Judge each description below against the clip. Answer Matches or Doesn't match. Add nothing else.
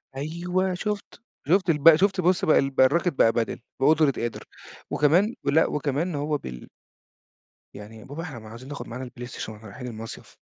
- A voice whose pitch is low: Doesn't match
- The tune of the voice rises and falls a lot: Matches